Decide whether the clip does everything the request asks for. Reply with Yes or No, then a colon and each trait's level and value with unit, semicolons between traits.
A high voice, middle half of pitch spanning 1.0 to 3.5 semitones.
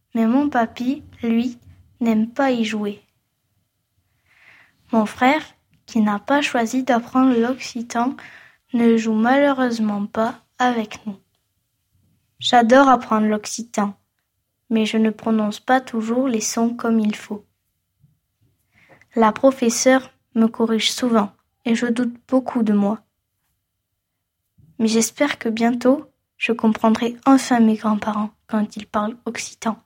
Yes: high, 225 Hz; average, 2.8 semitones